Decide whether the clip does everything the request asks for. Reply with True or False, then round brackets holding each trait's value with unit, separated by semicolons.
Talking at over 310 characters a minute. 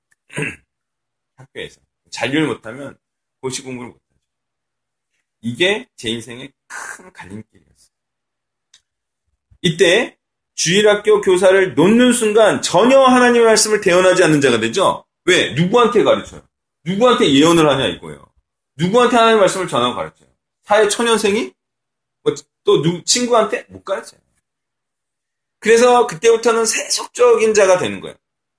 False (295 characters per minute)